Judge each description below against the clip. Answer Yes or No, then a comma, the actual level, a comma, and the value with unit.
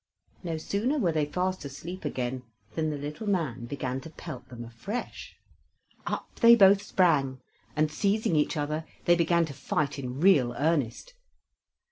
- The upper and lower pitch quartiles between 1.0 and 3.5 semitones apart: No, average, 5.2 semitones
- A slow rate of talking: No, average, 155 wpm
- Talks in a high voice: No, medium, 155 Hz